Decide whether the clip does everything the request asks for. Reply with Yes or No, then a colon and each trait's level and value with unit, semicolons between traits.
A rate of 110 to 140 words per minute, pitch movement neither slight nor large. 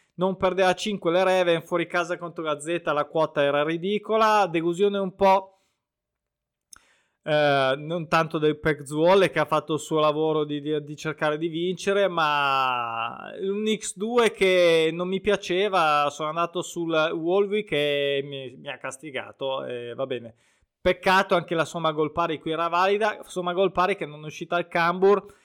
No: average, 165 wpm; average, 3.8 semitones